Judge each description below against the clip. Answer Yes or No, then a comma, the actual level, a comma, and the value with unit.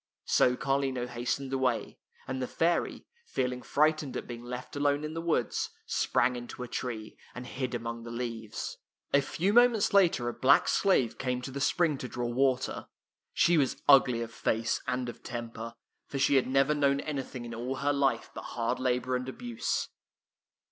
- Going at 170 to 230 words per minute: Yes, average, 180 wpm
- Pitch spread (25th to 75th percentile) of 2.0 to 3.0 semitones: Yes, average, 2.7 semitones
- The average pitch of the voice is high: No, low, 130 Hz